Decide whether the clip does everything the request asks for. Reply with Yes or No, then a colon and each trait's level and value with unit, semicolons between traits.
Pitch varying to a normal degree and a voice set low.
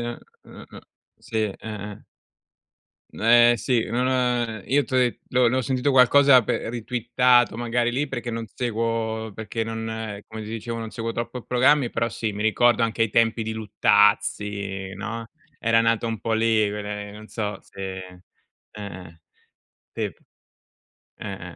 No: narrow, 2.3 semitones; low, 115 Hz